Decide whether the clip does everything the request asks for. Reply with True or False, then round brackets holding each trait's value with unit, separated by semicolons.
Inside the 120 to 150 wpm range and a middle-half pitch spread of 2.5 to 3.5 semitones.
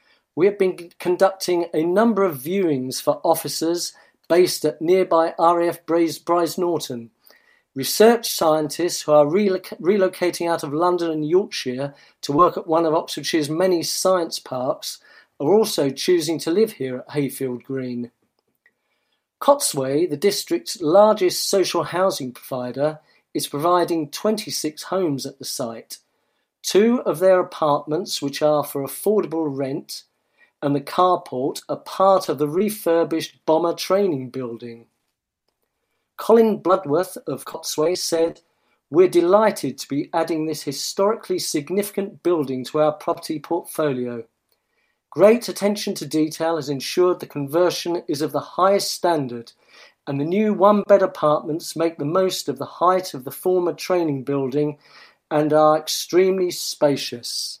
False (135 wpm; 4.1 semitones)